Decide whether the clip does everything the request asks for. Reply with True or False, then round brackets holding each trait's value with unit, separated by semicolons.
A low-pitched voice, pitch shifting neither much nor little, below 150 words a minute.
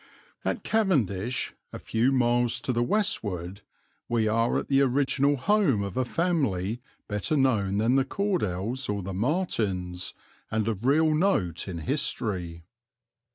False (120 Hz; 5.9 semitones; 140 wpm)